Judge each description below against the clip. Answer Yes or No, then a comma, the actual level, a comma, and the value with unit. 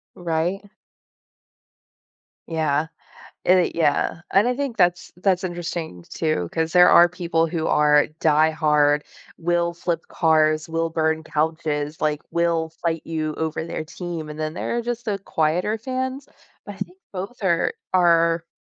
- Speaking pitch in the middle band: Yes, medium, 165 Hz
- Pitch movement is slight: Yes, narrow, 2.3 semitones